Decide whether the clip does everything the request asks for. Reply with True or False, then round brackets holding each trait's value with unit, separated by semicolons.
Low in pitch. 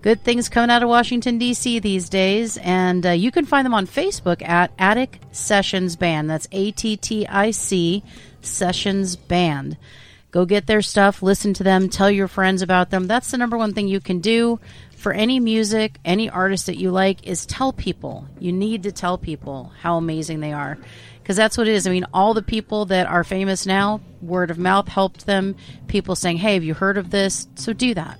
False (195 Hz)